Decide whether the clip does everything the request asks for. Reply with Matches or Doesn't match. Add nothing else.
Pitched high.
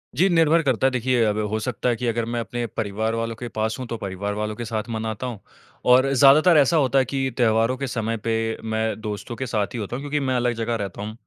Doesn't match